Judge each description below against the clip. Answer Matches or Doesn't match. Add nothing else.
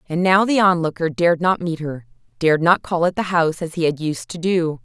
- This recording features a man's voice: Doesn't match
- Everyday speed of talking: Doesn't match